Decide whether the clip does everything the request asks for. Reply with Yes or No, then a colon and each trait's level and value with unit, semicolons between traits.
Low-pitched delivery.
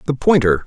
Yes: low, 130 Hz